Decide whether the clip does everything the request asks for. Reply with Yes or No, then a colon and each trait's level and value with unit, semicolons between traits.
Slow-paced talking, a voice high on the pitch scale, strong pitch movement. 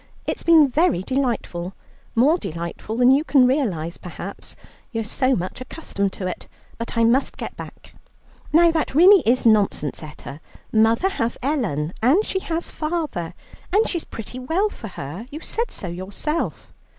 No: average, 160 wpm; high, 245 Hz; wide, 8.6 semitones